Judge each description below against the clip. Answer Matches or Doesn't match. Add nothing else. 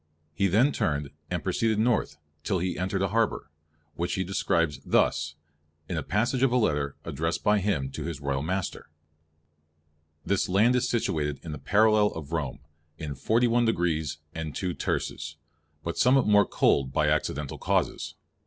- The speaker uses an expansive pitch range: Matches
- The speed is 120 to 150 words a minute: Doesn't match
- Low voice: Matches